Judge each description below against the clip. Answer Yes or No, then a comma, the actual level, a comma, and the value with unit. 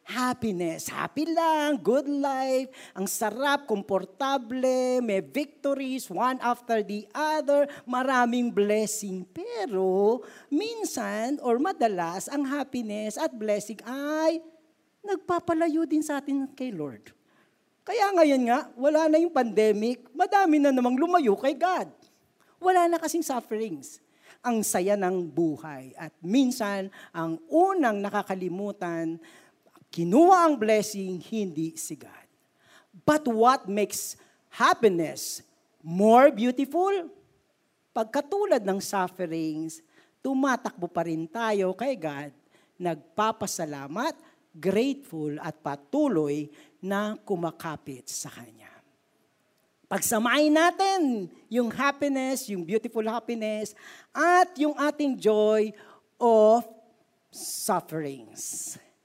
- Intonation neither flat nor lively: No, wide, 6.8 semitones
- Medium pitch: No, high, 235 Hz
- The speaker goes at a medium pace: No, slow, 100 wpm